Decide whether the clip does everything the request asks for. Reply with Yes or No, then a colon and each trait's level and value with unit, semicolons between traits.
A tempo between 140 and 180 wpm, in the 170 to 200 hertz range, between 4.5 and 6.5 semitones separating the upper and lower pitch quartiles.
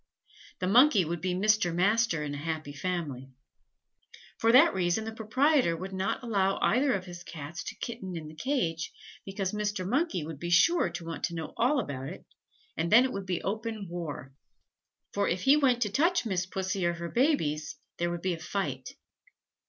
No: average, 190 wpm; medium, 185 Hz; average, 5.0 semitones